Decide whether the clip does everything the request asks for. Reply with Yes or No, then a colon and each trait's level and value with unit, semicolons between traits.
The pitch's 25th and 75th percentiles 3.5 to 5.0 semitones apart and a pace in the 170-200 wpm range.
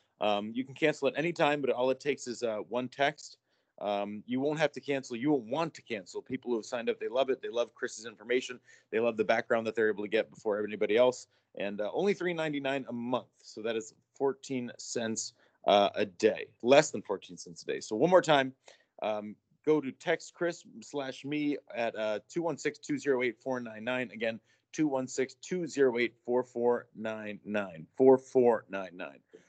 Yes: average, 4.4 semitones; average, 185 wpm